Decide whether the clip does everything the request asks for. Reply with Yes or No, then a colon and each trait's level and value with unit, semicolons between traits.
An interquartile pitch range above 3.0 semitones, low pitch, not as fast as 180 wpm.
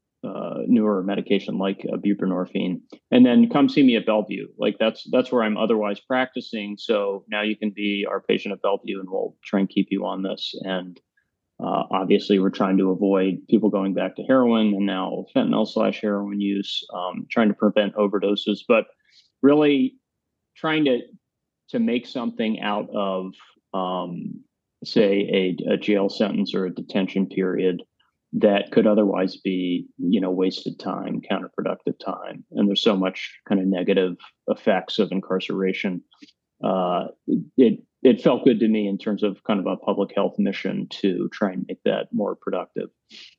No: narrow, 2.6 semitones; low, 100 Hz; average, 170 wpm